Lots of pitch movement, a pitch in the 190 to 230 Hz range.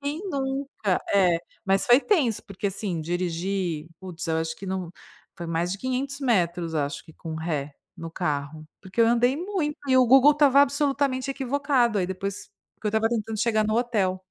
Yes: wide, 7.1 semitones; high, 205 Hz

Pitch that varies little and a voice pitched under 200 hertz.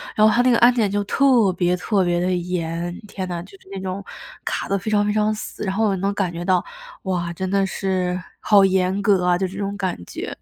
Yes: narrow, 2.3 semitones; high, 190 Hz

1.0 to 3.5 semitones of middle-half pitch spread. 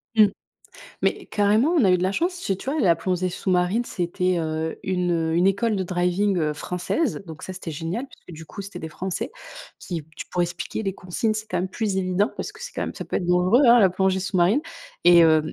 Yes: average, 2.9 semitones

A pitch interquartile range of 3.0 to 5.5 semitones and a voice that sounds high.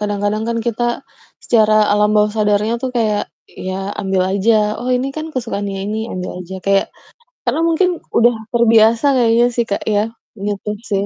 No: narrow, 2.6 semitones; high, 215 Hz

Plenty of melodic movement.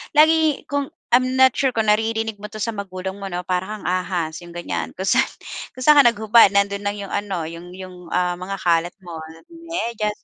No: average, 4.2 semitones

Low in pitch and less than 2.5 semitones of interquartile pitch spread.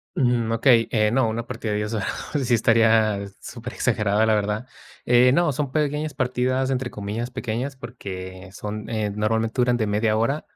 No: low, 115 Hz; average, 2.9 semitones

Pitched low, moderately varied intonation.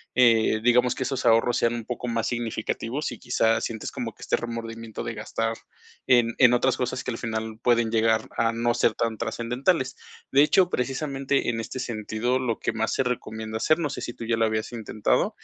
No: low, 115 Hz; narrow, 1.9 semitones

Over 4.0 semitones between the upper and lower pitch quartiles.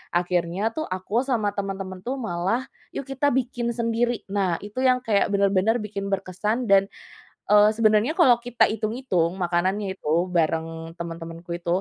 Yes: average, 4.8 semitones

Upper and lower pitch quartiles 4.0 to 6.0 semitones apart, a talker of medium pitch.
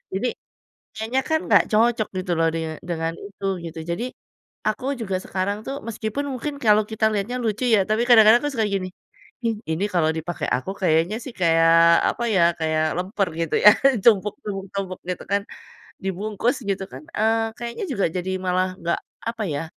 No: average, 4.4 semitones; high, 200 Hz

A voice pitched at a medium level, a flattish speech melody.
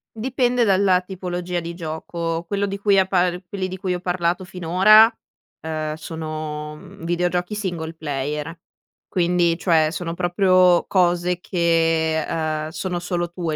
Yes: medium, 175 Hz; narrow, 2.3 semitones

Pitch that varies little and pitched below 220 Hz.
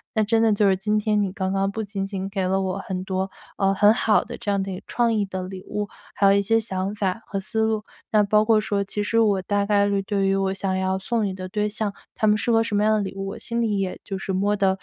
Yes: narrow, 1.7 semitones; high, 200 Hz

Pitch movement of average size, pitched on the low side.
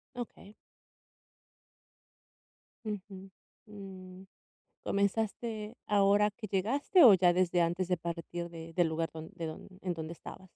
No: average, 3.3 semitones; high, 190 Hz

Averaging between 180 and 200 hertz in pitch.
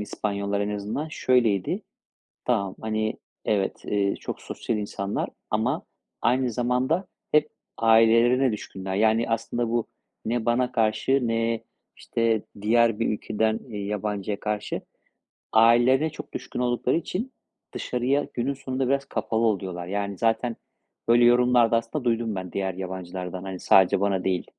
No: low, 115 Hz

